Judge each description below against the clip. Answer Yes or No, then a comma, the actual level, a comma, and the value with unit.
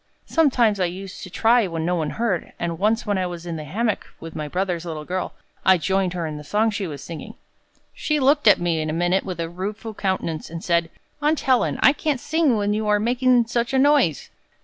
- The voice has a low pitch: No, high, 190 Hz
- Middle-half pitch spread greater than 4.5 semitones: Yes, wide, 5.6 semitones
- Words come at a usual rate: No, fast, 230 wpm